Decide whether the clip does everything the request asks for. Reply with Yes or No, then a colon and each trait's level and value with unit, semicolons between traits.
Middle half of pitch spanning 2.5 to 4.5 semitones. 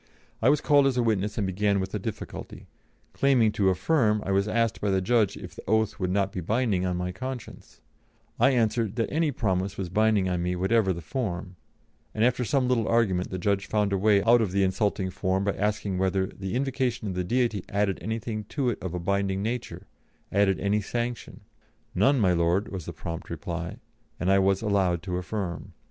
Yes: average, 3.4 semitones